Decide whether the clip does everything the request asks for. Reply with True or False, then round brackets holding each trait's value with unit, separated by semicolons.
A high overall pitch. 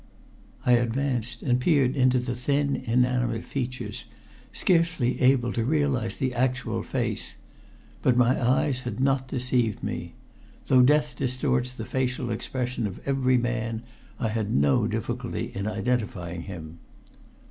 False (125 Hz)